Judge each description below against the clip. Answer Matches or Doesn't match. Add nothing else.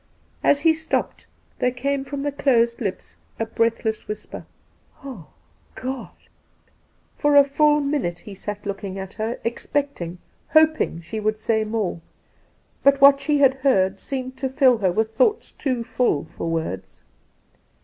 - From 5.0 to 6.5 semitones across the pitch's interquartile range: Matches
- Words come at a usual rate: Matches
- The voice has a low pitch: Doesn't match